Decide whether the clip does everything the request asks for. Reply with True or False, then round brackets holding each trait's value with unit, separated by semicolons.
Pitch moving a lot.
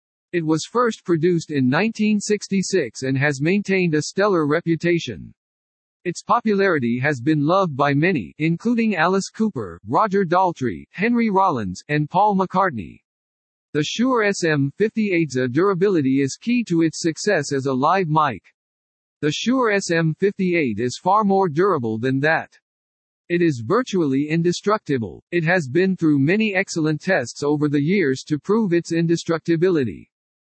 True (5.7 semitones)